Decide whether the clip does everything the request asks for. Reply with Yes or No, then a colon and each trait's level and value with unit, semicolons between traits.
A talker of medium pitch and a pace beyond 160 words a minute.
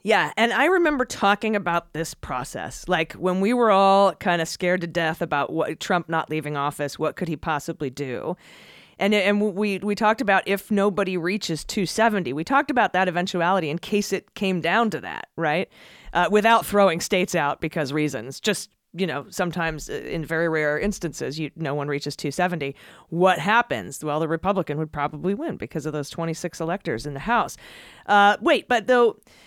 Yes: medium, 175 Hz; average, 190 wpm